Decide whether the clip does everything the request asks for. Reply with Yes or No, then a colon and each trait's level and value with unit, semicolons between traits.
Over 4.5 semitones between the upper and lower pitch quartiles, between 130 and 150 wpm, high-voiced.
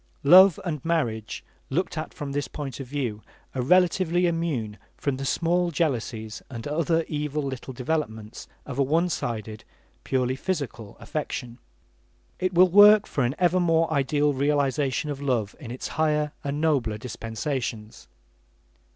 No: average, 4.9 semitones; average, 145 wpm; medium, 145 Hz